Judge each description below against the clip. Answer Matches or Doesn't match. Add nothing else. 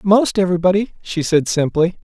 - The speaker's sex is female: Doesn't match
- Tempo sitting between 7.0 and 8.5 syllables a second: Doesn't match